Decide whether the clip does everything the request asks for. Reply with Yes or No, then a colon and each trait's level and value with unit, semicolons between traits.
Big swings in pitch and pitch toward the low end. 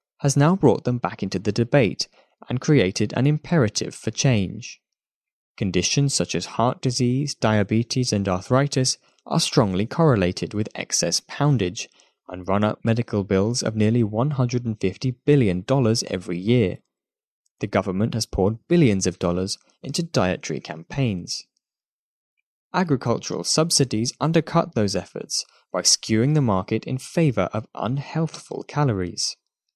Yes: wide, 5.9 semitones; low, 115 Hz